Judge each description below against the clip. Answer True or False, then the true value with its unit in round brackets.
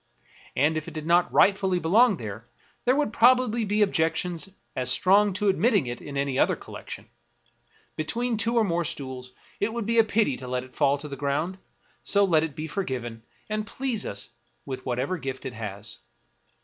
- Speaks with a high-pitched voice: False (165 Hz)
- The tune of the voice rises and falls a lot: True (7.8 semitones)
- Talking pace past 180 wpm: True (190 wpm)